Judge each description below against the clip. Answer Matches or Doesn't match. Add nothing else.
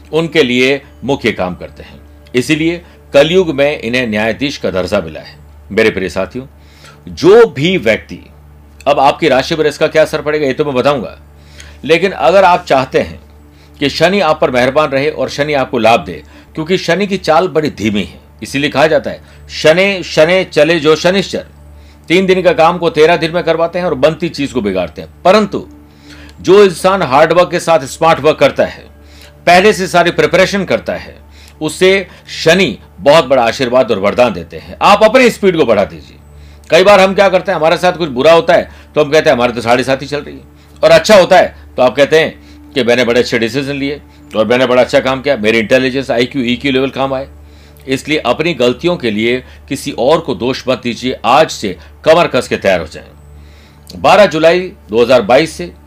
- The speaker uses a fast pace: Matches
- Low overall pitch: Matches